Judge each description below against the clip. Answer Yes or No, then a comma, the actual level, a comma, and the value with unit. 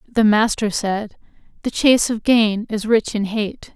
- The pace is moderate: Yes, average, 175 wpm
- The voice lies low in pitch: No, high, 215 Hz